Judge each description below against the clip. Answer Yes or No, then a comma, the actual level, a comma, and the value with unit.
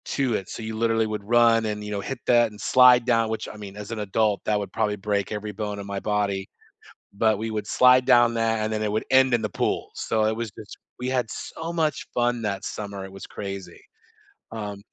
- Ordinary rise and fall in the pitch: No, narrow, 2.3 semitones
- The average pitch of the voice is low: Yes, low, 110 Hz